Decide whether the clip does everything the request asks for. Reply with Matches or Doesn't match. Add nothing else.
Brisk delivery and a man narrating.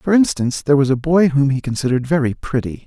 Matches